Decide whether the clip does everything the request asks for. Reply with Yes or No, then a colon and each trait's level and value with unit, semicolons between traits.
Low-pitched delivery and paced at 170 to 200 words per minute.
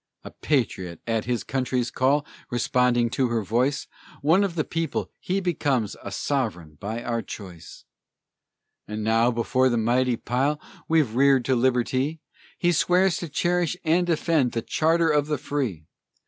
No: low, 130 Hz; average, 155 wpm